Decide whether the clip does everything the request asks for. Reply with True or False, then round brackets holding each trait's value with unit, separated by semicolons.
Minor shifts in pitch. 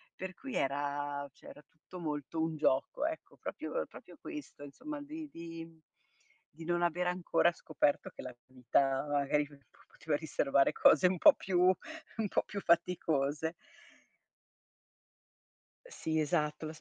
False (4.0 semitones)